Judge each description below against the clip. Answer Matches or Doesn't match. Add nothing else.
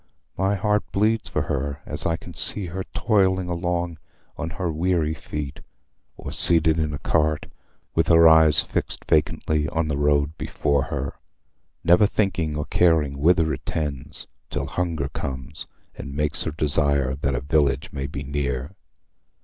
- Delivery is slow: Doesn't match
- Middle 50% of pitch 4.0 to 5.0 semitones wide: Doesn't match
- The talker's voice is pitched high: Doesn't match